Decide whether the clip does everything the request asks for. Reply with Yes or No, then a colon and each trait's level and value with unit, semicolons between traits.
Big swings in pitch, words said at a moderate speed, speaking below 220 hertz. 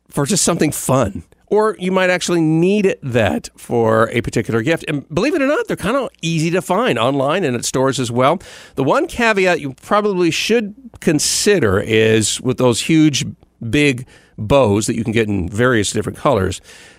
Yes: wide, 7.8 semitones; average, 185 wpm; medium, 140 Hz